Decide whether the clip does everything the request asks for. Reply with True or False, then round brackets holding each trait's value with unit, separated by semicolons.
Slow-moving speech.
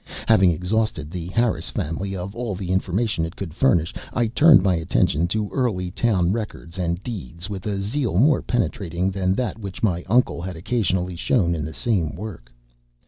False (180 wpm)